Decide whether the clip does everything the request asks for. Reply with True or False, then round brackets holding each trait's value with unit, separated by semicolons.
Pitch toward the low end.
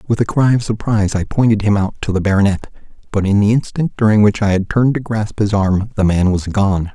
True (105 Hz)